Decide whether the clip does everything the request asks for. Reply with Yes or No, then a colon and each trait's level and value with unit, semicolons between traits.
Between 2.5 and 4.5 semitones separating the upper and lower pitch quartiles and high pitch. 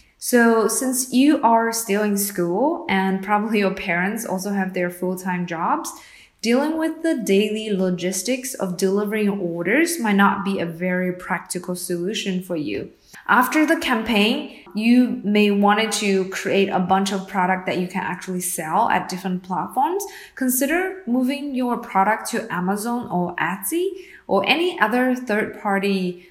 No: average, 5.1 semitones; high, 205 Hz